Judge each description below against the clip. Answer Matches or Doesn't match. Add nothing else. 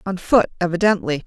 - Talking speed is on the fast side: Doesn't match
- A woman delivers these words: Matches